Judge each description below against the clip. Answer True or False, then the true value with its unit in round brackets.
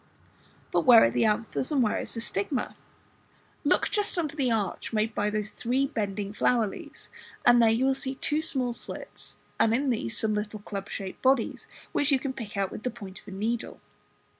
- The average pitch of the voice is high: True (225 Hz)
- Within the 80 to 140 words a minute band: False (205 wpm)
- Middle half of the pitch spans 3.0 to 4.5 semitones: True (4.0 semitones)